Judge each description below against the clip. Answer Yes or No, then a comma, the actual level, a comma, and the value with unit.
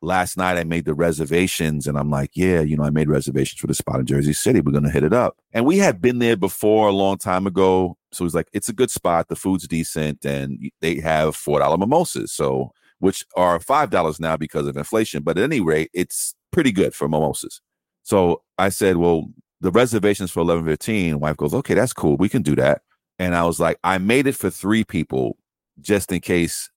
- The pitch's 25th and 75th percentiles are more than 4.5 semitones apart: No, average, 3.8 semitones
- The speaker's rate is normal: No, fast, 225 wpm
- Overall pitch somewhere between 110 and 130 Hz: No, very low, 85 Hz